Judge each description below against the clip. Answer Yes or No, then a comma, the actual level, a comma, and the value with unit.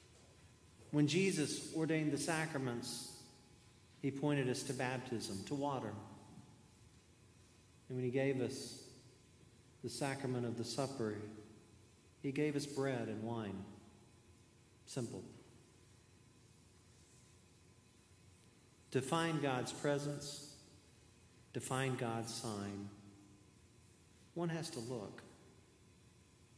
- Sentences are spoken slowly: Yes, slow, 95 wpm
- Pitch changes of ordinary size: Yes, average, 4.2 semitones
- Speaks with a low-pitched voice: Yes, low, 115 Hz